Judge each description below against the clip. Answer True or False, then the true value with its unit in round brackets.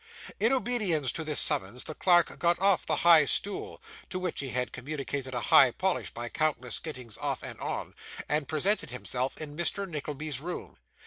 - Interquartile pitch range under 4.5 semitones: False (5.2 semitones)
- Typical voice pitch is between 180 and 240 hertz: False (155 Hz)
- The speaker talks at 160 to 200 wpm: True (180 wpm)